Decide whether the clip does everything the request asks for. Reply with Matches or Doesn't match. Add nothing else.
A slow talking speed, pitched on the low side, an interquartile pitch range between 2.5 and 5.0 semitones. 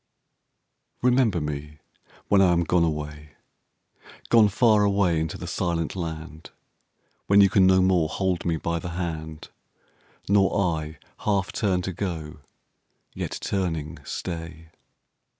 Matches